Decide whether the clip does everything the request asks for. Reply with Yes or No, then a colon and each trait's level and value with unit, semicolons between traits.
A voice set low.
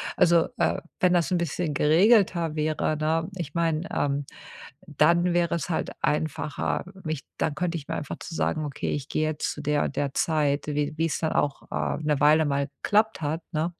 No: medium, 155 Hz